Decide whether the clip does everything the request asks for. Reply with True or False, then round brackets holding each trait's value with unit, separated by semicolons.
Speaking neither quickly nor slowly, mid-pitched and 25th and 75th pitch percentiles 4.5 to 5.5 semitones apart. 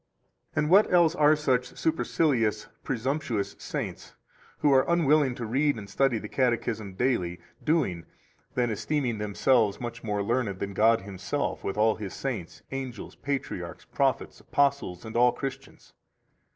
False (145 wpm; 125 Hz; 4.8 semitones)